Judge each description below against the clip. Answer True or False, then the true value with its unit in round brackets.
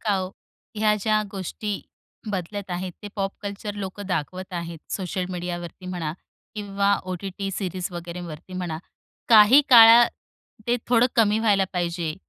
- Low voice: False (190 Hz)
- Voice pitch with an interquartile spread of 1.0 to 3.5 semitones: True (2.8 semitones)